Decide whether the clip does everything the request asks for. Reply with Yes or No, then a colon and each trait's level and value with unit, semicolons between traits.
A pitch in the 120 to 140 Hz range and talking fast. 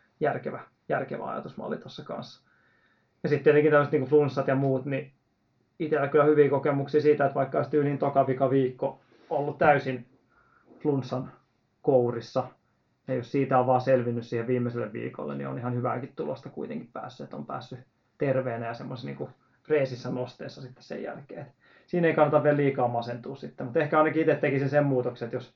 Yes: low, 135 Hz; fast, 170 wpm